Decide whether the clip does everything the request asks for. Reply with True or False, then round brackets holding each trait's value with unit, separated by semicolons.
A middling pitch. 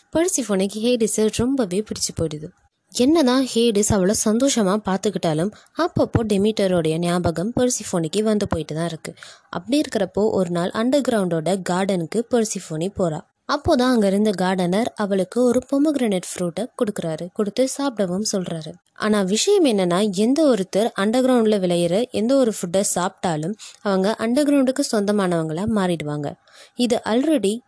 False (210 Hz)